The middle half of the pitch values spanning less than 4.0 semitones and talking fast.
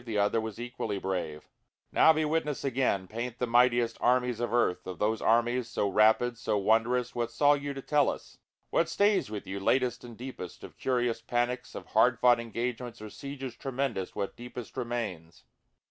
No: narrow, 2.4 semitones; average, 180 wpm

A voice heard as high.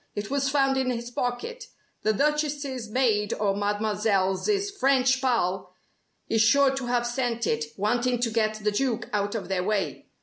Yes: high, 235 Hz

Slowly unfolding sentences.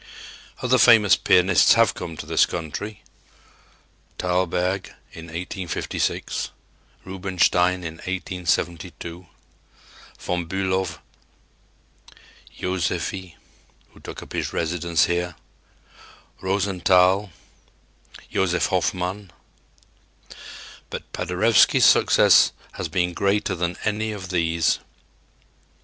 Yes: slow, 85 wpm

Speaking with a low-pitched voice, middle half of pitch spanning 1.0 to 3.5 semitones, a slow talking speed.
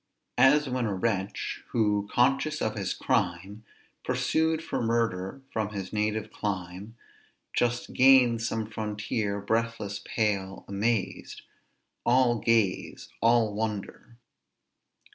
Yes: low, 110 Hz; average, 2.8 semitones; slow, 105 wpm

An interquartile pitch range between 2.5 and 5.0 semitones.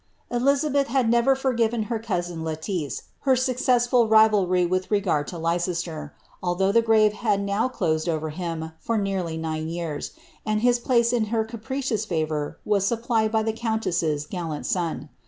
No: wide, 5.6 semitones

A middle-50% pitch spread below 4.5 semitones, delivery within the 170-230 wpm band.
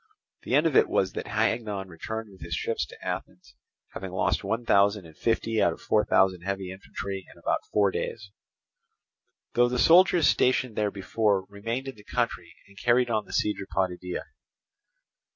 Yes: average, 3.4 semitones; average, 180 wpm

